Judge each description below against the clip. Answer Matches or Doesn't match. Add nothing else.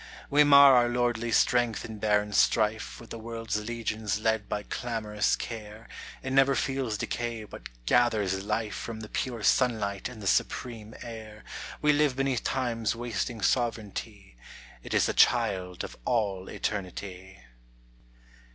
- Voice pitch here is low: Matches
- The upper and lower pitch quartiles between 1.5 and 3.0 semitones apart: Matches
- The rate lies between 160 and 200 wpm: Doesn't match